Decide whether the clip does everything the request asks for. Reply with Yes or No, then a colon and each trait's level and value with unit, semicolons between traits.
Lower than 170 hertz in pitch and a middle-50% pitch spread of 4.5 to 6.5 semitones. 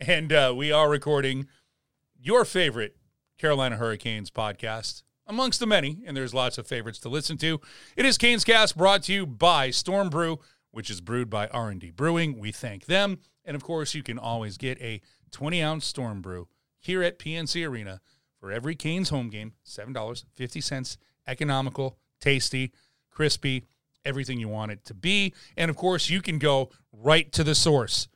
Yes: medium, 140 Hz; average, 5.2 semitones